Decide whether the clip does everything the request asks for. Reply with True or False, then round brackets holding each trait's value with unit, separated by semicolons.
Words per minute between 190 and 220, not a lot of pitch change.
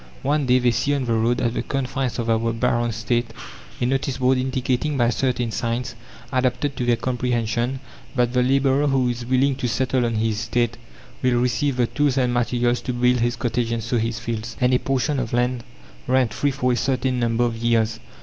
True (205 wpm; 1.8 semitones)